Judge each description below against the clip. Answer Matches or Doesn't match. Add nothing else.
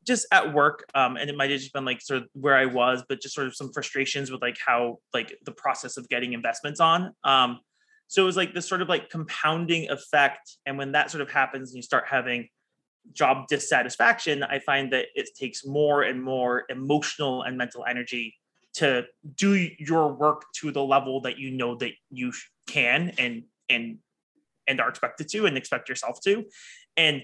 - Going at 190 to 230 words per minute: Matches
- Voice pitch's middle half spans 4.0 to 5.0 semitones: Doesn't match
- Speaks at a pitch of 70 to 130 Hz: Doesn't match